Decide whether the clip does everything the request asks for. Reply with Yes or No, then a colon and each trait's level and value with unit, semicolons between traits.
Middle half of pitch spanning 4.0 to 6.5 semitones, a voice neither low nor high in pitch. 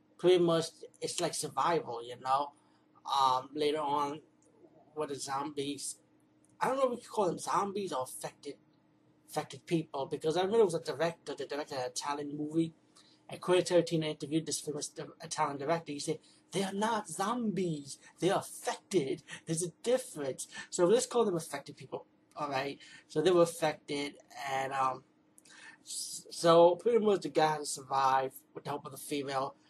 No: average, 3.3 semitones; medium, 155 Hz